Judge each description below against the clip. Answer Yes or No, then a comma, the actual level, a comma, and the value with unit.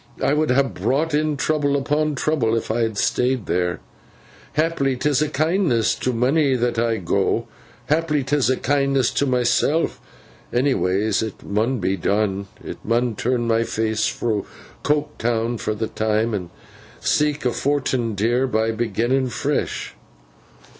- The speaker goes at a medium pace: Yes, average, 145 wpm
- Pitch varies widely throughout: No, average, 4.3 semitones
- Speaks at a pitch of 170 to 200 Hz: No, low, 125 Hz